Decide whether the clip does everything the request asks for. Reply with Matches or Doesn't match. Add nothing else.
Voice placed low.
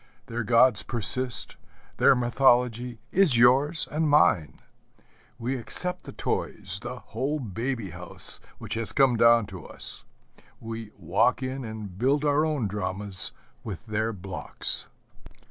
Matches